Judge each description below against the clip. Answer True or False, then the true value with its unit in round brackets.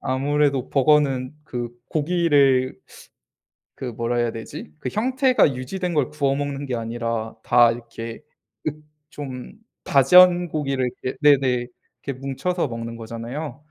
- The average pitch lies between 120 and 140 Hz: True (135 Hz)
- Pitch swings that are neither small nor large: True (3.7 semitones)